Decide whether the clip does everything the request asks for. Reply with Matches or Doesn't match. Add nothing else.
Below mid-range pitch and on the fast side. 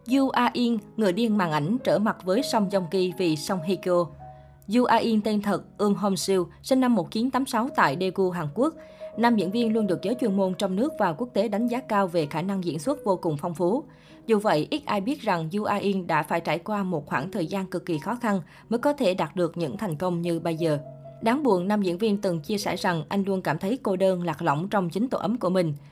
Doesn't match